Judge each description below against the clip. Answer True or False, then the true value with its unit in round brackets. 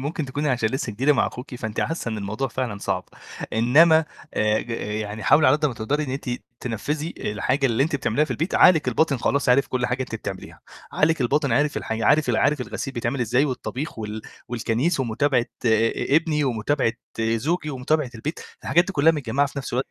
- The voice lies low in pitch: True (130 Hz)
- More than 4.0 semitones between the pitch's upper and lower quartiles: True (4.5 semitones)